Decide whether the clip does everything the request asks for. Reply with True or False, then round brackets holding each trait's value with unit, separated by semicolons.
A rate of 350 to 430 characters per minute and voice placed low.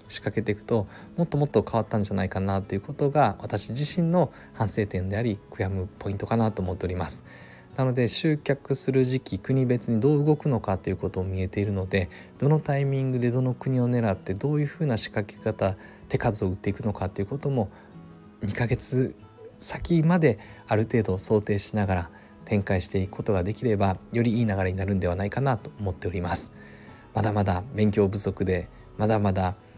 True (405 characters per minute; 110 Hz)